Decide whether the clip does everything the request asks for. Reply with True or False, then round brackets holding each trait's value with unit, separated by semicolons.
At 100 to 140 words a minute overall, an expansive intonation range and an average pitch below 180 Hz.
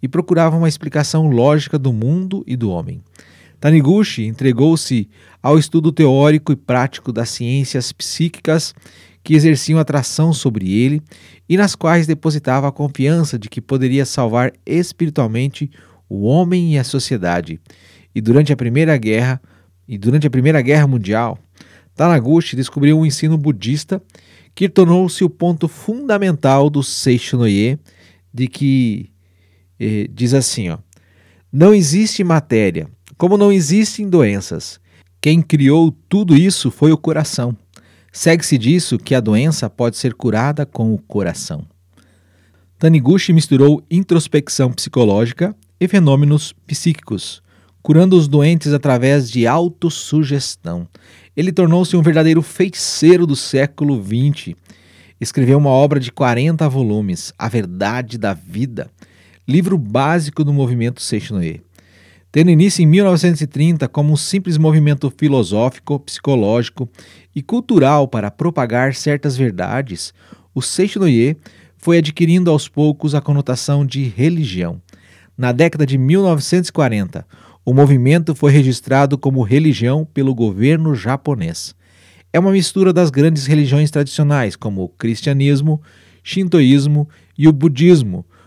True (125 wpm; 5.7 semitones; 140 Hz)